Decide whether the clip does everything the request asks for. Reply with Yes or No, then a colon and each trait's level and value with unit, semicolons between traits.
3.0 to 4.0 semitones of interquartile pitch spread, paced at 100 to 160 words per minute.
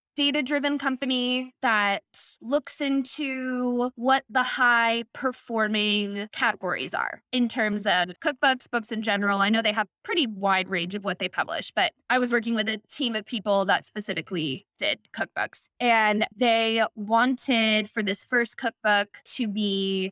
Yes: average, 3.7 semitones; average, 155 wpm